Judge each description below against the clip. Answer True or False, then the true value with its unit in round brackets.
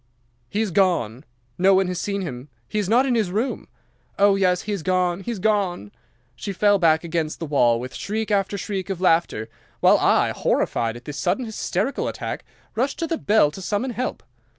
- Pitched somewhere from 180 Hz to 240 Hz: True (190 Hz)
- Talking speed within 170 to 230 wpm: True (200 wpm)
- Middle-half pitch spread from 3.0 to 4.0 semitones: False (4.5 semitones)